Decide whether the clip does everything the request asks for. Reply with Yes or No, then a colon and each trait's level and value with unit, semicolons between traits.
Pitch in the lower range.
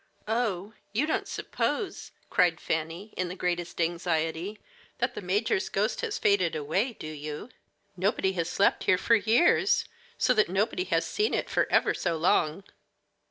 No: medium, 185 Hz